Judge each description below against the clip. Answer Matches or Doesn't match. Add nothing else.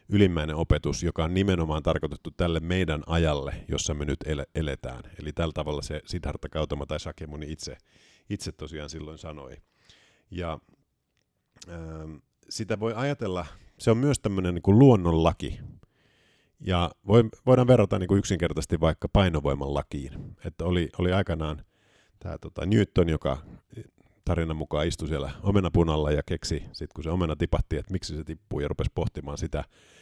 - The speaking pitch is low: Matches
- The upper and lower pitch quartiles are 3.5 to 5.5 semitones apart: Matches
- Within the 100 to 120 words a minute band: Doesn't match